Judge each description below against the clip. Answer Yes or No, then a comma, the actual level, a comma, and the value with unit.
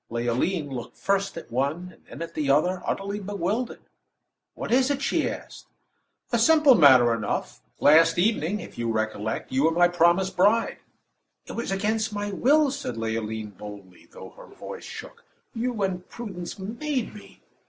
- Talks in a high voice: No, medium, 180 Hz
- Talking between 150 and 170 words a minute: Yes, average, 165 wpm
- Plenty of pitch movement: Yes, wide, 8.8 semitones